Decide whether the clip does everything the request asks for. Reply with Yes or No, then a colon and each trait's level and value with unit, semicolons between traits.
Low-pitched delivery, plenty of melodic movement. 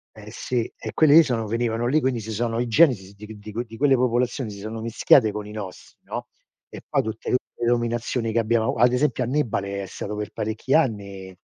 No: low, 115 Hz; average, 2.7 semitones